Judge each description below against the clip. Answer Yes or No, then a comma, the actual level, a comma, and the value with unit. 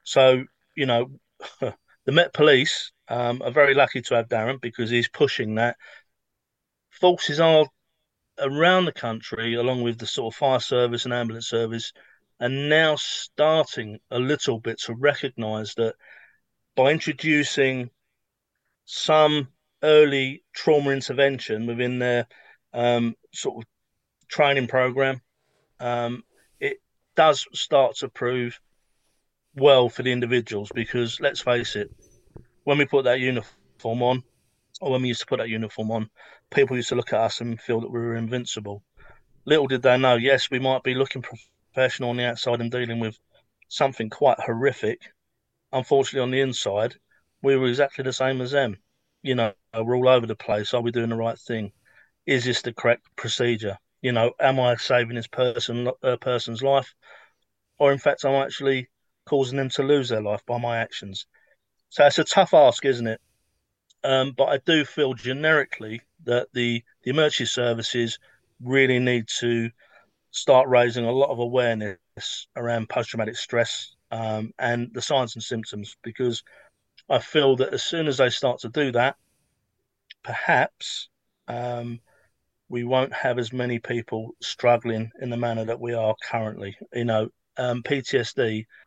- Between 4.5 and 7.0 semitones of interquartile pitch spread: No, narrow, 2.6 semitones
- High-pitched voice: No, low, 120 Hz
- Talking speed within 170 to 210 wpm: No, average, 160 wpm